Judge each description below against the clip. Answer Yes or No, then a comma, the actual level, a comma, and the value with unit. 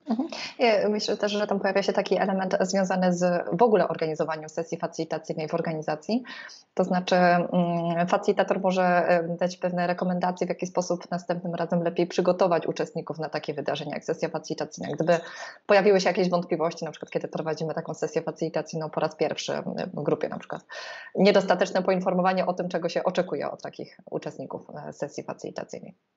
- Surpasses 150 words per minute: Yes, fast, 160 wpm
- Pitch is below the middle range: No, medium, 175 Hz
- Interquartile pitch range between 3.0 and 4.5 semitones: No, narrow, 2.5 semitones